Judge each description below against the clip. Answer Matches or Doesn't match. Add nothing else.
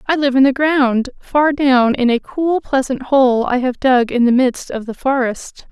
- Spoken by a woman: Matches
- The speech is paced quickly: Matches